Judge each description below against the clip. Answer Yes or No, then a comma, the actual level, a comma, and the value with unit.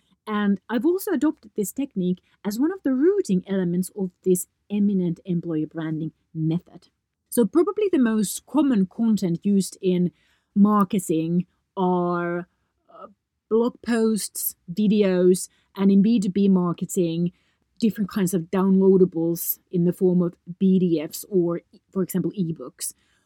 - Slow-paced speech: Yes, slow, 125 wpm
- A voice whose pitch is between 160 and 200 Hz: Yes, high, 190 Hz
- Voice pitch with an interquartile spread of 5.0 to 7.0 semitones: No, average, 3.2 semitones